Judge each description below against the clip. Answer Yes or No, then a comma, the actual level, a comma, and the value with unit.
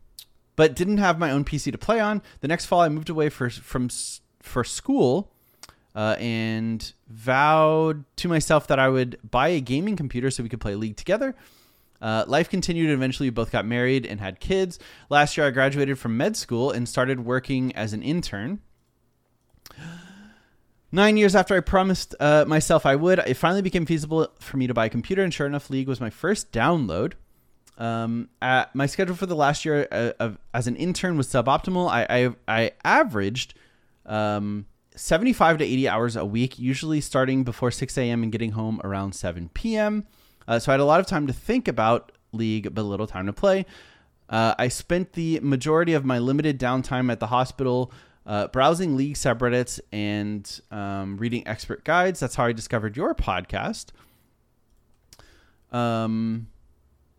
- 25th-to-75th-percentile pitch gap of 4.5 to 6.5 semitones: Yes, wide, 5.6 semitones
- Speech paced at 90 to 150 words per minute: No, average, 180 wpm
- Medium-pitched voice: No, low, 130 Hz